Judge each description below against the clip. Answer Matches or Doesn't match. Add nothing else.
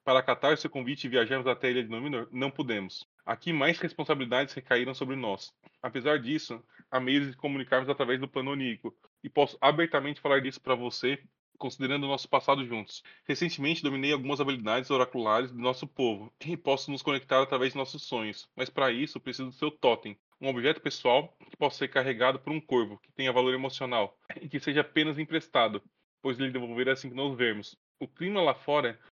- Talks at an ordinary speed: Doesn't match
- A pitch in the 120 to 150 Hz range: Matches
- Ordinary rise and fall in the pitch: Doesn't match